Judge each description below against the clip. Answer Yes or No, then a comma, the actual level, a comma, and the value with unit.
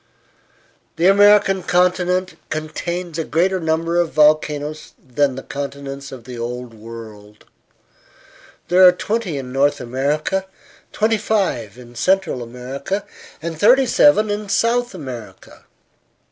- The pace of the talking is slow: Yes, slow, 120 wpm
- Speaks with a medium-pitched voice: Yes, medium, 155 Hz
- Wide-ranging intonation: Yes, wide, 6.7 semitones